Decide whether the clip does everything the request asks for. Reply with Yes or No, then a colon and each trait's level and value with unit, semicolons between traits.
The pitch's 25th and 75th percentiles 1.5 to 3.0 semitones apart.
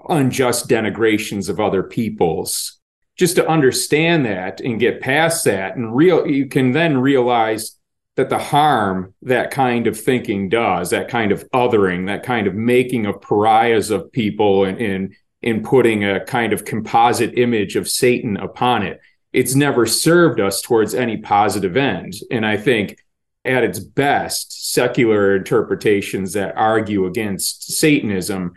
No: average, 4.8 semitones